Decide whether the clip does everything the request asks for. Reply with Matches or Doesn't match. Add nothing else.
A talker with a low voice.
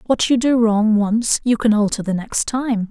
Doesn't match